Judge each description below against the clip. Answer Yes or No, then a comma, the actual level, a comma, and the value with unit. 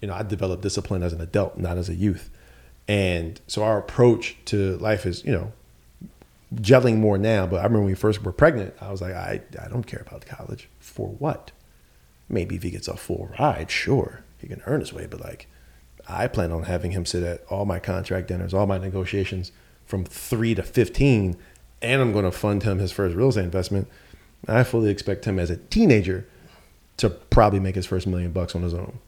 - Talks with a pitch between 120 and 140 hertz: No, very low, 95 Hz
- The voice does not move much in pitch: No, average, 3.3 semitones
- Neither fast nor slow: No, fast, 215 wpm